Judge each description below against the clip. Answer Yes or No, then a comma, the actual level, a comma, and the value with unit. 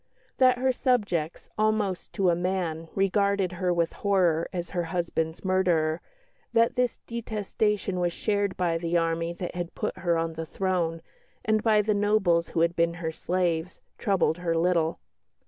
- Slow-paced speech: No, average, 165 wpm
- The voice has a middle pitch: Yes, medium, 180 Hz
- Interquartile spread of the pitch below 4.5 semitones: Yes, average, 3.2 semitones